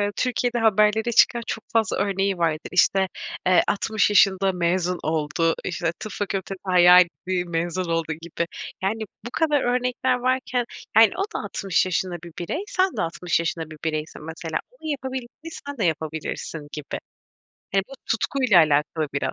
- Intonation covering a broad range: Yes, wide, 6.1 semitones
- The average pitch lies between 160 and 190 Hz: Yes, medium, 185 Hz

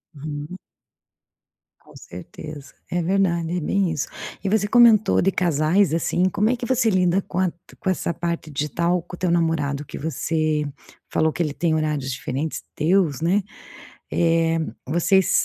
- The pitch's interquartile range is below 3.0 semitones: No, average, 3.5 semitones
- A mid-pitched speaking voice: Yes, medium, 170 Hz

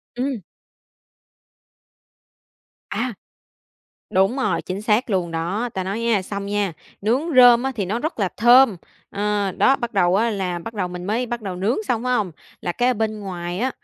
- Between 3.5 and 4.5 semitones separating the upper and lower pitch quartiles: Yes, average, 4.1 semitones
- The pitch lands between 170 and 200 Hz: No, high, 210 Hz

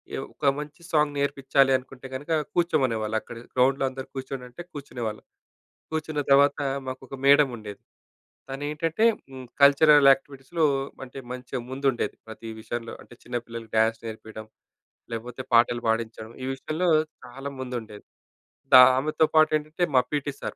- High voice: No, low, 135 Hz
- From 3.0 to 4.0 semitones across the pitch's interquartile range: Yes, average, 3.5 semitones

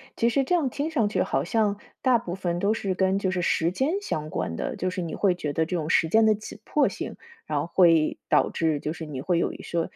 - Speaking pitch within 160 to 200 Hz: Yes, medium, 185 Hz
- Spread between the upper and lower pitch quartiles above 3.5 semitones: Yes, average, 5.2 semitones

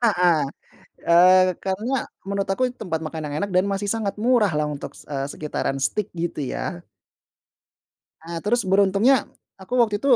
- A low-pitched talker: No, high, 195 Hz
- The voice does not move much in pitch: No, average, 3.8 semitones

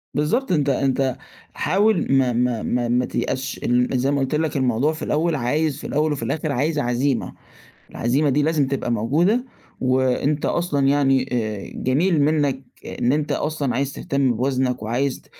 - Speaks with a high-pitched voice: No, medium, 140 Hz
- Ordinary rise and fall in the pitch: Yes, average, 3.2 semitones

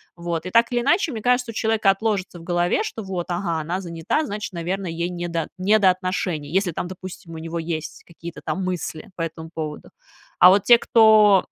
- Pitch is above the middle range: No, medium, 180 Hz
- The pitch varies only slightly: No, average, 3.7 semitones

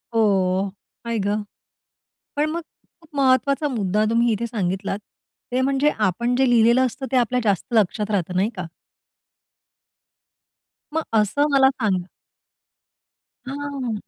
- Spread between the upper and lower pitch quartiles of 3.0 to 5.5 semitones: Yes, average, 4.7 semitones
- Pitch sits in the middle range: No, high, 230 Hz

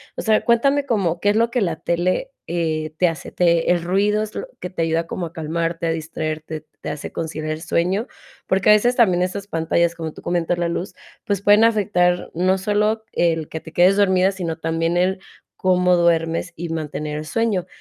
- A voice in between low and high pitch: Yes, medium, 175 Hz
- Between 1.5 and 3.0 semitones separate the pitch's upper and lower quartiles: No, average, 3.4 semitones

